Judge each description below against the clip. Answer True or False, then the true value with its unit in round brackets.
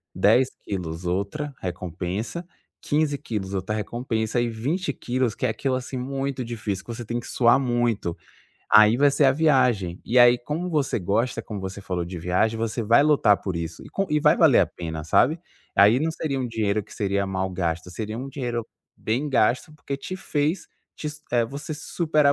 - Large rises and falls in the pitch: True (5.8 semitones)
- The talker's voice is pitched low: True (120 Hz)